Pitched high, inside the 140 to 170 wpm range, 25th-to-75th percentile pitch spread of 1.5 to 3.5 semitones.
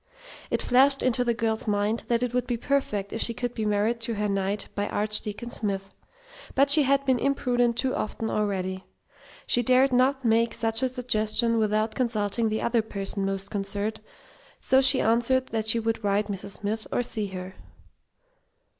No: high, 225 Hz; average, 180 wpm; average, 3.1 semitones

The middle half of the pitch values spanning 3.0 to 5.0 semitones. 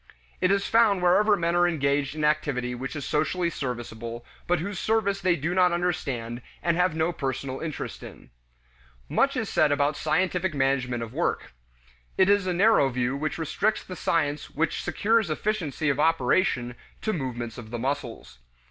No: wide, 5.4 semitones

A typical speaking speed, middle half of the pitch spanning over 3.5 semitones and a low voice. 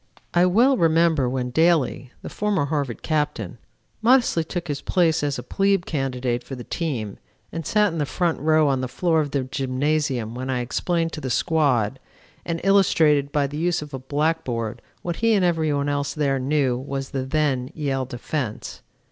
No: average, 185 wpm; average, 4.0 semitones; medium, 145 Hz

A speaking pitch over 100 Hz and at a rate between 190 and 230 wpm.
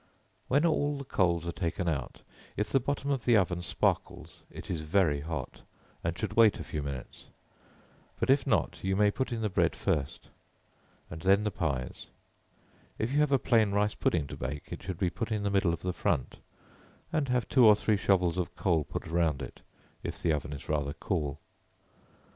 No: very low, 95 Hz; average, 200 wpm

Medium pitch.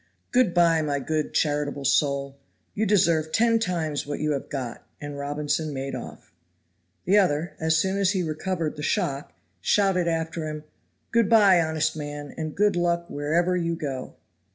Yes: medium, 160 Hz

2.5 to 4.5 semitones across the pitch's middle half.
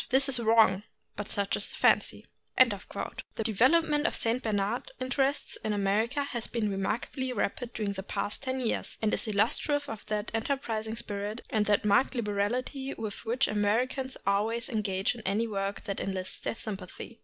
Yes: average, 3.7 semitones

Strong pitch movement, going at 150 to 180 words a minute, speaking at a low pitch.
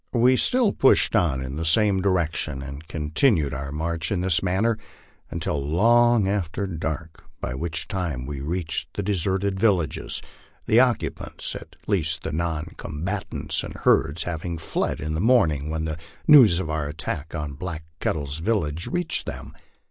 No: average, 4.5 semitones; average, 160 wpm; very low, 85 Hz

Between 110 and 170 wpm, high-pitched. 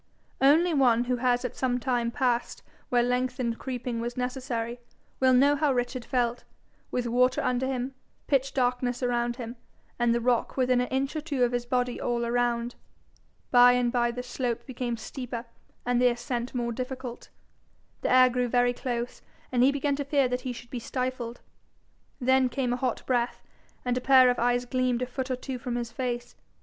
No: average, 185 wpm; very high, 250 Hz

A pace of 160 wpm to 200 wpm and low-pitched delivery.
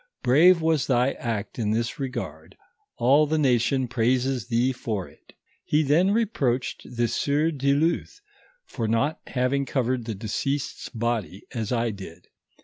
No: average, 145 wpm; low, 125 Hz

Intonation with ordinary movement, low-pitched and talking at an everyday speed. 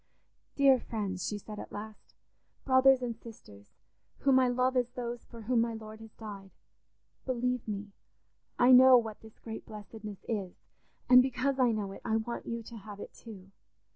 No: average, 3.0 semitones; high, 230 Hz; average, 175 wpm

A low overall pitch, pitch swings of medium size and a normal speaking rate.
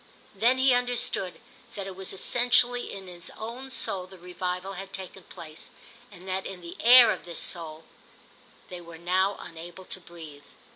No: high, 190 Hz; average, 4.4 semitones; average, 165 wpm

